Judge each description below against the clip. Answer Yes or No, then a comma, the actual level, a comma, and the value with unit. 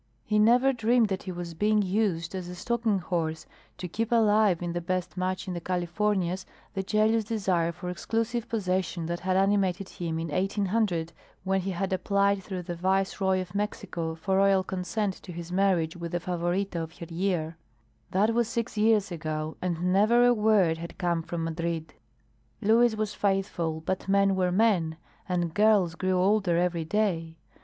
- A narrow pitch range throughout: No, average, 3.3 semitones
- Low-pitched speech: No, medium, 185 Hz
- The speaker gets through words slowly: No, average, 175 wpm